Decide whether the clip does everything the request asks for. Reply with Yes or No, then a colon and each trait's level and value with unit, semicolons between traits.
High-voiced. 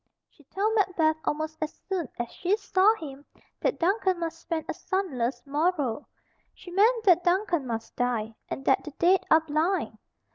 Yes: very high, 330 Hz